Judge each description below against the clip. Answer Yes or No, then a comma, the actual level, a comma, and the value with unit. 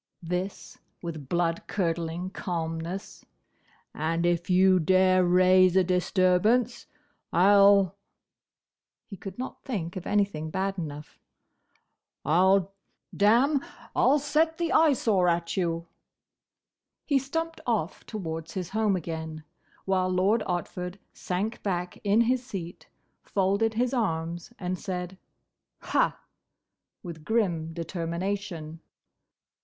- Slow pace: Yes, slow, 110 wpm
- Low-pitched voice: No, medium, 185 Hz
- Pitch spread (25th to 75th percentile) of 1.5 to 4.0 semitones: Yes, average, 3.3 semitones